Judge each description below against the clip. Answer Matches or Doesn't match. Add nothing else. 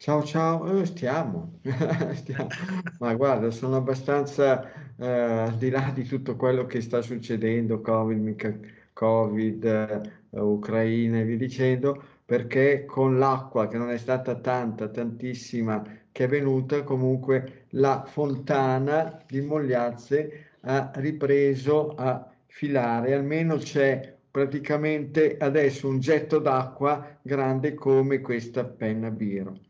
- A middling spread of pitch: Matches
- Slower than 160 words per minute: Matches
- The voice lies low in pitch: Matches